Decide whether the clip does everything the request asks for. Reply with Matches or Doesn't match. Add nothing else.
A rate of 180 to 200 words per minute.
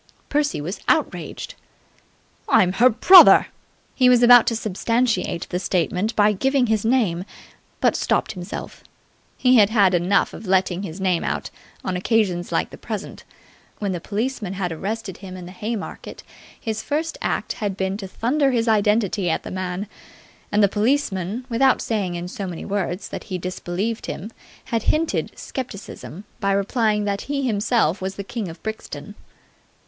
Doesn't match